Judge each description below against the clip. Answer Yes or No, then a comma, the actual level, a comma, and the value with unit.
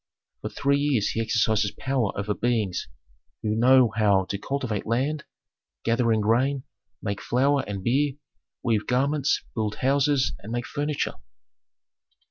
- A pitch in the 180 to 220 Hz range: No, low, 120 Hz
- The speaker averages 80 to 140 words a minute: Yes, slow, 135 wpm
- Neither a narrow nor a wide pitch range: Yes, average, 4.3 semitones